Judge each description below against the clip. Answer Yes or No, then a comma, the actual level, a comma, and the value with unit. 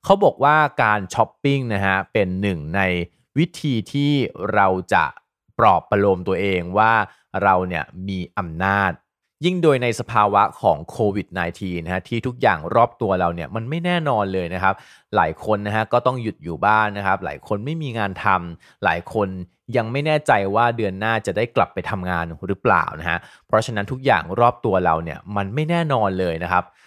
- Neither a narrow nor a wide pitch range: Yes, average, 4.5 semitones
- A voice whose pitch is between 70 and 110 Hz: Yes, low, 100 Hz